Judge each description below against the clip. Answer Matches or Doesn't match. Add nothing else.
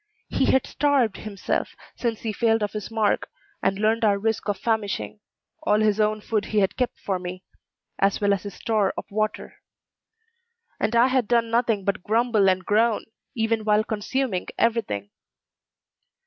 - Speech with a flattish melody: Matches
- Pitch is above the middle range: Matches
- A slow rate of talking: Doesn't match